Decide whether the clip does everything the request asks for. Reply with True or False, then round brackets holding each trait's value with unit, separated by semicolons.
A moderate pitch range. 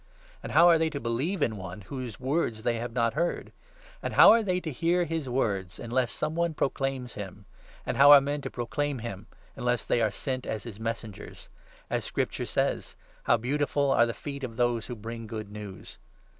True (4.4 semitones)